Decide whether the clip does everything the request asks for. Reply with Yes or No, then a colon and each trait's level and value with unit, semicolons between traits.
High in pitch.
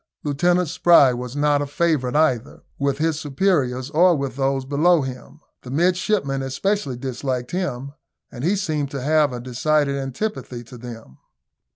No: medium, 140 Hz